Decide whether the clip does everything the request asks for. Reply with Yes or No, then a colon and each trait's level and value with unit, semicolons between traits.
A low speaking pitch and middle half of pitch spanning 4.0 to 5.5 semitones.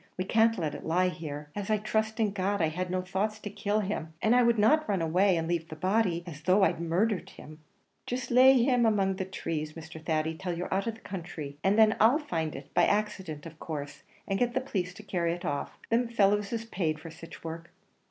No: high, 190 Hz; average, 4.8 semitones